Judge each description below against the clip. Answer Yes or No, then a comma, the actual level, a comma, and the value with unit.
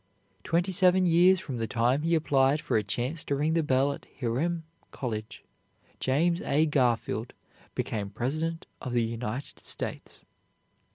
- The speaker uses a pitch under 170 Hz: Yes, medium, 140 Hz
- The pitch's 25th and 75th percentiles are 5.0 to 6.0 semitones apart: Yes, wide, 5.5 semitones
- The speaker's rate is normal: Yes, average, 150 wpm